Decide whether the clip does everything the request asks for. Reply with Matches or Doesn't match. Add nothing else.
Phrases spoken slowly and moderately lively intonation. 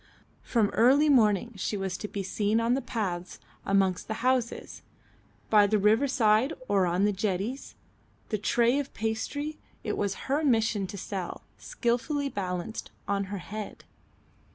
Doesn't match